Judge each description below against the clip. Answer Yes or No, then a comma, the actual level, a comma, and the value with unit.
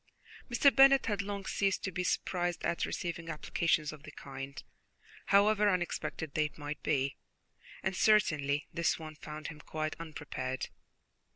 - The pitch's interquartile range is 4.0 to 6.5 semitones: Yes, average, 4.5 semitones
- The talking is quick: No, average, 145 wpm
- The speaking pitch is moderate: Yes, medium, 165 Hz